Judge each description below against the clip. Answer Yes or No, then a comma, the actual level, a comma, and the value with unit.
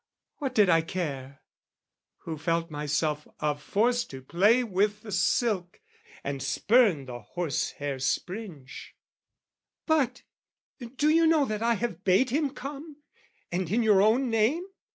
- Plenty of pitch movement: Yes, wide, 7.9 semitones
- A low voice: No, high, 200 Hz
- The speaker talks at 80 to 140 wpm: Yes, slow, 135 wpm